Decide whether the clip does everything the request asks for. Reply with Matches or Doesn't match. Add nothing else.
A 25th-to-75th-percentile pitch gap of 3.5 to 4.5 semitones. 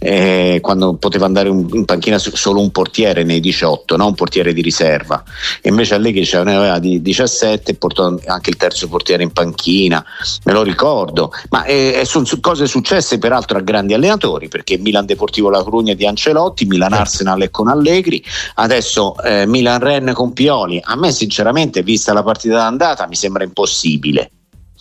Matches